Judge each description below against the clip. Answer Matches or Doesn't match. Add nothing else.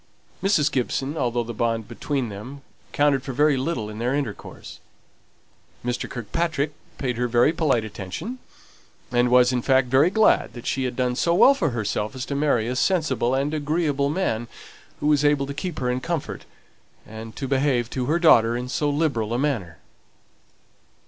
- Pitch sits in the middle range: Doesn't match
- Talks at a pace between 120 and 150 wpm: Doesn't match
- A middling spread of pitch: Matches